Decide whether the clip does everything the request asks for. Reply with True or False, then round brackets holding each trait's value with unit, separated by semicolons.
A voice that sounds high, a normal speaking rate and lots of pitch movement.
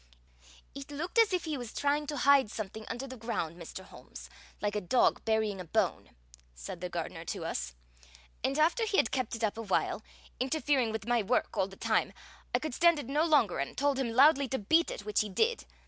False (245 Hz; 215 wpm; 6.1 semitones)